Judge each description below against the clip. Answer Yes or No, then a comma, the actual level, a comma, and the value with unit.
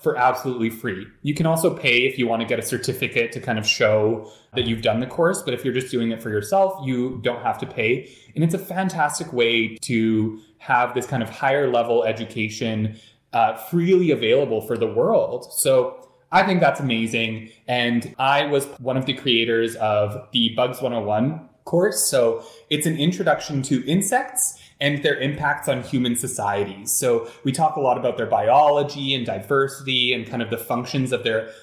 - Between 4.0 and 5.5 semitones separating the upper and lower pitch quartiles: Yes, average, 4.5 semitones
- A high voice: No, low, 130 Hz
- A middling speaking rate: Yes, average, 190 wpm